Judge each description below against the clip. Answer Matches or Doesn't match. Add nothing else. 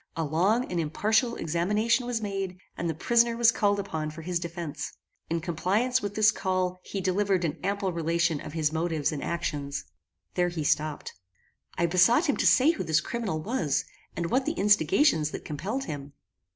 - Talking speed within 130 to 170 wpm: Doesn't match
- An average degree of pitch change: Matches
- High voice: Doesn't match